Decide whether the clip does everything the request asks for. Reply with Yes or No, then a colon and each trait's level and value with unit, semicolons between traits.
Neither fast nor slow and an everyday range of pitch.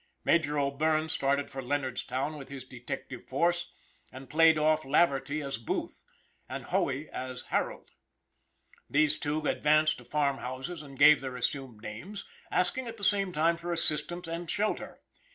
Yes: average, 155 wpm; average, 3.5 semitones